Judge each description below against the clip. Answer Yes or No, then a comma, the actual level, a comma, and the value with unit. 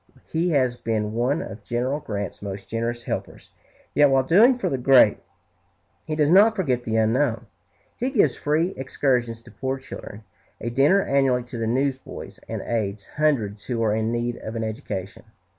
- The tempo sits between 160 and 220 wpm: Yes, average, 175 wpm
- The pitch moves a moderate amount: Yes, average, 4.3 semitones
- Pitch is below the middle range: Yes, low, 125 Hz